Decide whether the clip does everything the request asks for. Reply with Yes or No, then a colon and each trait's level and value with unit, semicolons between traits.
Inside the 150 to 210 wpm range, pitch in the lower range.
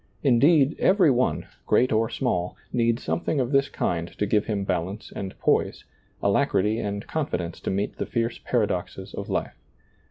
Yes: average, 160 wpm; low, 115 Hz